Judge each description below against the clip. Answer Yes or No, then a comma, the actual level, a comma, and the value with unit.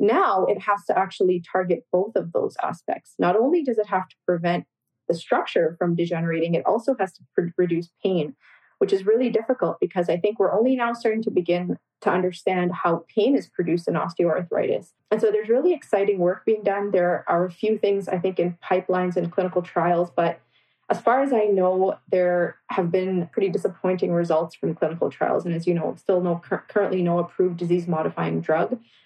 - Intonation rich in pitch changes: No, average, 2.9 semitones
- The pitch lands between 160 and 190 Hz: Yes, medium, 185 Hz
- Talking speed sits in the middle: Yes, average, 195 wpm